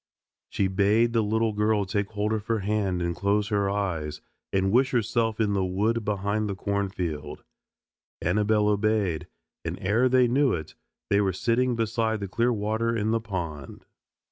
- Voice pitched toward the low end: Yes, low, 105 Hz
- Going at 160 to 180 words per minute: Yes, average, 170 wpm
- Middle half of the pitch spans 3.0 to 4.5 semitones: No, narrow, 2.5 semitones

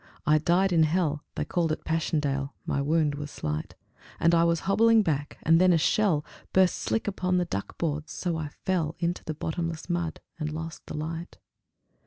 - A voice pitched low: No, medium, 165 Hz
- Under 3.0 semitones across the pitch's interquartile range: Yes, narrow, 2.6 semitones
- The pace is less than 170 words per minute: No, average, 190 wpm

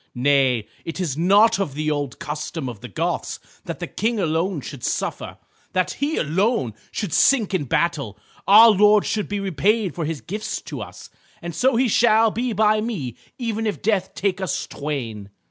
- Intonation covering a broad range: Yes, wide, 6.7 semitones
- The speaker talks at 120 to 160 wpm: No, average, 180 wpm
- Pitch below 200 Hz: Yes, medium, 185 Hz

